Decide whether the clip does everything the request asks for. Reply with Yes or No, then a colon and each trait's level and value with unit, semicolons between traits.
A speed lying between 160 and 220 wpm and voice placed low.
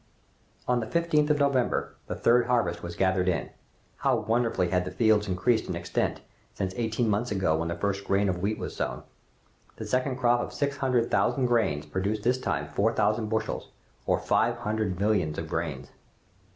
Yes: average, 185 wpm; low, 110 Hz